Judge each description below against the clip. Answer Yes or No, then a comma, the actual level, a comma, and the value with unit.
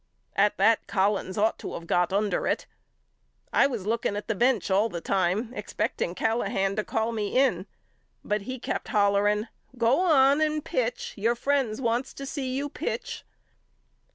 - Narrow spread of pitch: No, average, 4.2 semitones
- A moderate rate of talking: Yes, average, 170 wpm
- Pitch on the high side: Yes, high, 220 Hz